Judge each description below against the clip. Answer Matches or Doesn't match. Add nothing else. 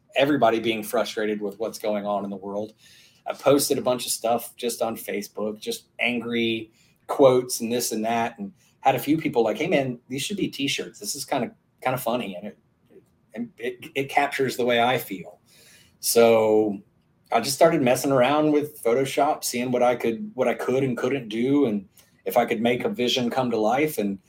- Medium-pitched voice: Doesn't match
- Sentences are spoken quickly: Matches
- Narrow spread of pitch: Doesn't match